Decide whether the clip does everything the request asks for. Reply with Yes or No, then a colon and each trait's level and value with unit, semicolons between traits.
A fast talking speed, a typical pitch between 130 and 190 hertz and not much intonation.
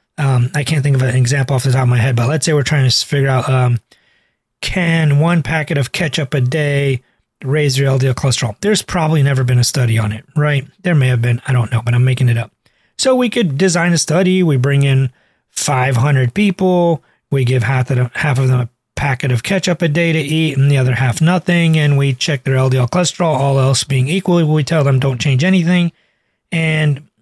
No: fast, 225 wpm; medium, 140 Hz; average, 3.8 semitones